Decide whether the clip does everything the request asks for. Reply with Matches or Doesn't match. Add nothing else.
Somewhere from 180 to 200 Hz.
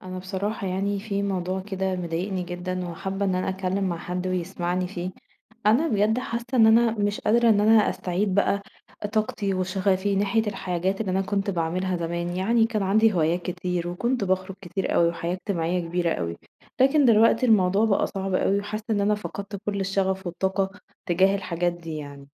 Matches